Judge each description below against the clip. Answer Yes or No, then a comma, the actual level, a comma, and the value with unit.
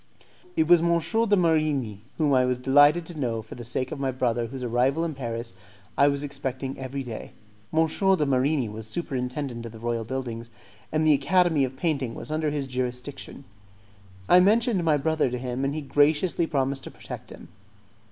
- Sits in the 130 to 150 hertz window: Yes, medium, 140 Hz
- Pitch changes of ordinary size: Yes, average, 4.0 semitones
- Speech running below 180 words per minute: No, average, 190 wpm